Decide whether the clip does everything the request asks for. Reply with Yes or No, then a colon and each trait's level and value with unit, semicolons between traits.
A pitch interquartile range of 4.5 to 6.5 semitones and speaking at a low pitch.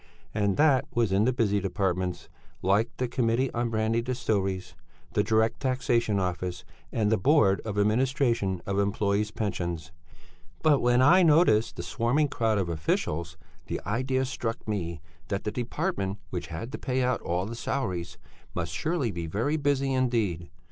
Yes: average, 5.1 semitones; low, 110 Hz